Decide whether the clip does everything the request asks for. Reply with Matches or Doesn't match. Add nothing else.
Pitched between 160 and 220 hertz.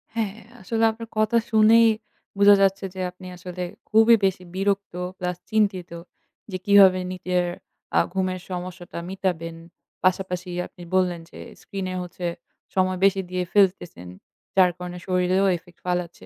Matches